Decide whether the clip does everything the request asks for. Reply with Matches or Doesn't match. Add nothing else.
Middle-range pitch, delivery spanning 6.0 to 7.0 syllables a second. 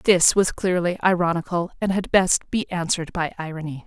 Doesn't match